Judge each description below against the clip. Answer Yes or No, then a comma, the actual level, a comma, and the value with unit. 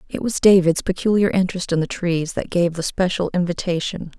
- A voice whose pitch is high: No, medium, 180 Hz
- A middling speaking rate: Yes, average, 185 wpm